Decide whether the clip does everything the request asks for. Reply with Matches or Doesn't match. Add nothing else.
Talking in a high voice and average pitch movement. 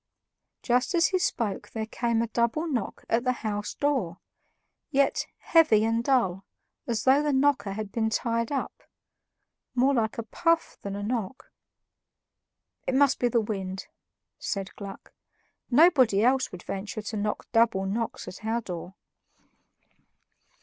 Matches